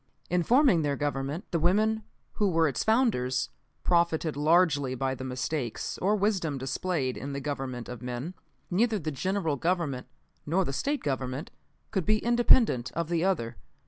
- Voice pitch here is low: No, medium, 160 Hz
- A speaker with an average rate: Yes, average, 160 wpm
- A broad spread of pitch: Yes, wide, 6.0 semitones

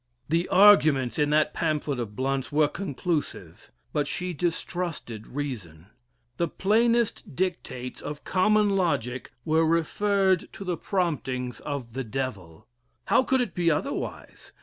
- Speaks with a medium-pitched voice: Yes, medium, 155 Hz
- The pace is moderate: No, slow, 130 wpm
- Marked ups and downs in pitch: Yes, wide, 6.0 semitones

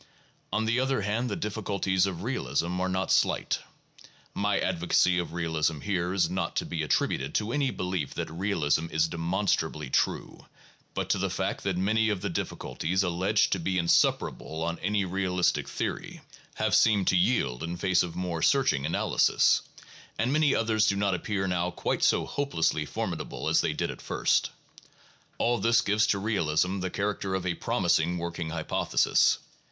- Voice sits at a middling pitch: No, very low, 95 Hz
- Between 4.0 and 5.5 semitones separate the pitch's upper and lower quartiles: No, average, 3.5 semitones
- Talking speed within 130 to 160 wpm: No, average, 170 wpm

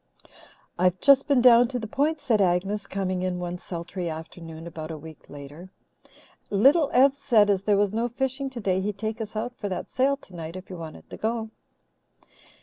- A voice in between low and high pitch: No, high, 205 Hz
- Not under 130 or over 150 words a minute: No, average, 195 wpm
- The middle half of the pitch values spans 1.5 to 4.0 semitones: No, wide, 5.6 semitones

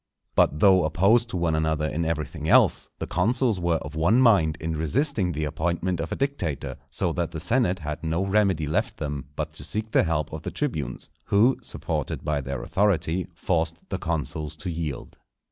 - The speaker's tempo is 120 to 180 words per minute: No, average, 190 wpm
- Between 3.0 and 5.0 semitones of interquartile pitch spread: Yes, average, 3.9 semitones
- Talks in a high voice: No, very low, 85 Hz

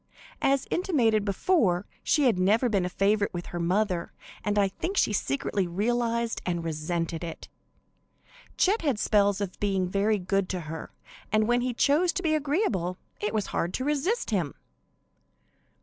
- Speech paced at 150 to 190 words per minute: Yes, average, 165 wpm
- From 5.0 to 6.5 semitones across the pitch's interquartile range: Yes, average, 5.3 semitones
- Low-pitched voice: No, high, 205 Hz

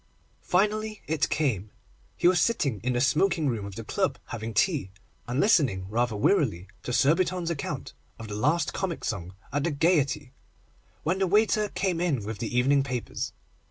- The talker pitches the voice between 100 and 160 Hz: Yes, medium, 140 Hz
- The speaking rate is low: No, average, 170 wpm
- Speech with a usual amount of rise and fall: No, wide, 7.7 semitones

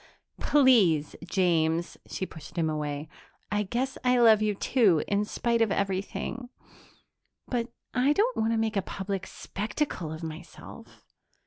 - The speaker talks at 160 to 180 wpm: No, average, 140 wpm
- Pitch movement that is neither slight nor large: No, wide, 5.9 semitones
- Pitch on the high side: Yes, high, 205 Hz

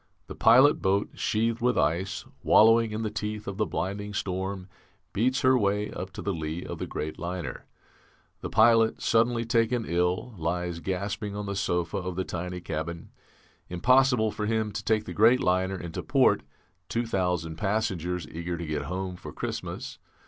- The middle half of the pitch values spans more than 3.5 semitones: Yes, average, 3.9 semitones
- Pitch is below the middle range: Yes, low, 100 Hz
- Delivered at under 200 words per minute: Yes, average, 170 wpm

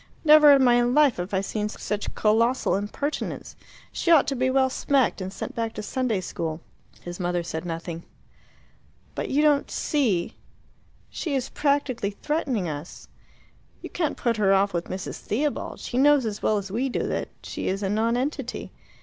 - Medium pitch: No, high, 230 Hz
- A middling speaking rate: Yes, average, 175 wpm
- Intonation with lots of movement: Yes, wide, 5.9 semitones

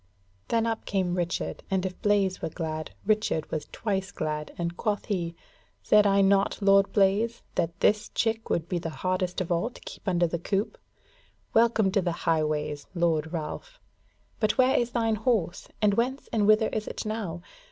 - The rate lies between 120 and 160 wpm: No, average, 180 wpm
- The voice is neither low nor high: No, high, 195 Hz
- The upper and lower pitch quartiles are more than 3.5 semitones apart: Yes, average, 4.2 semitones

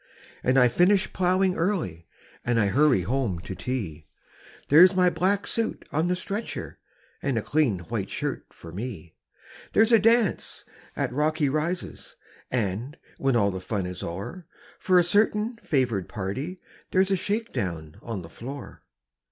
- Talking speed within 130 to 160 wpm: Yes, average, 155 wpm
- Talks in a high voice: No, medium, 140 Hz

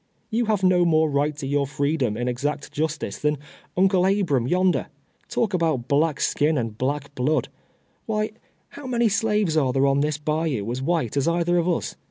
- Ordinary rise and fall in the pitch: Yes, average, 4.5 semitones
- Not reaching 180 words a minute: No, average, 185 wpm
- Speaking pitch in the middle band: Yes, medium, 155 Hz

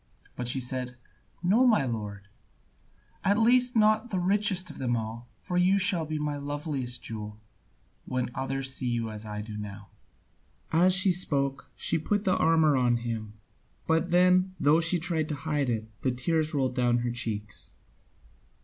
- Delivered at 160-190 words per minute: Yes, average, 170 wpm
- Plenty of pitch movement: Yes, wide, 6.8 semitones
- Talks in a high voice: No, medium, 140 Hz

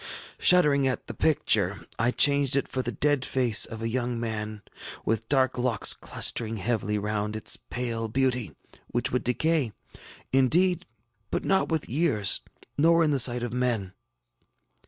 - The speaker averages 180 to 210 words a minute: No, average, 155 wpm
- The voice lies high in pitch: No, low, 125 Hz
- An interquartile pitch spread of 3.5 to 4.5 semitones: Yes, average, 3.9 semitones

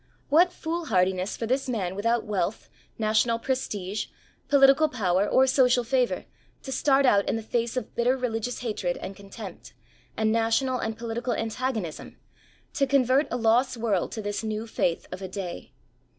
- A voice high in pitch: Yes, high, 230 Hz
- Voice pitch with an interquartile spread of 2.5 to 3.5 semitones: No, average, 3.9 semitones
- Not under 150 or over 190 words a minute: Yes, average, 160 wpm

